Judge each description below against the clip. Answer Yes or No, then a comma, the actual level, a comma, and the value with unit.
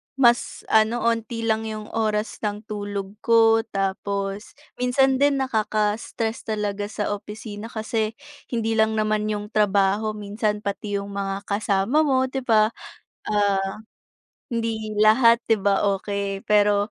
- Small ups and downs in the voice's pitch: Yes, narrow, 1.8 semitones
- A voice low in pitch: No, high, 215 Hz